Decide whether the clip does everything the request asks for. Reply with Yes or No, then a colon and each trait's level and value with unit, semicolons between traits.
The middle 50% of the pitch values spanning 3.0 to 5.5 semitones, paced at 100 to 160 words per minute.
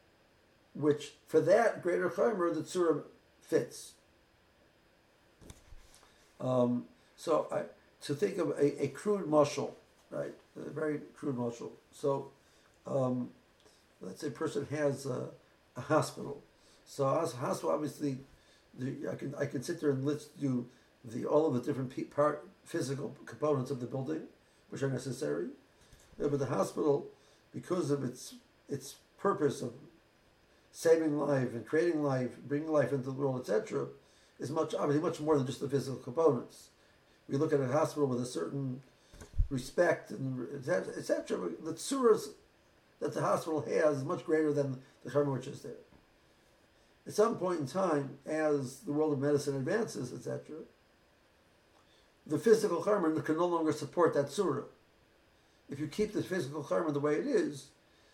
No: narrow, 2.5 semitones; average, 155 wpm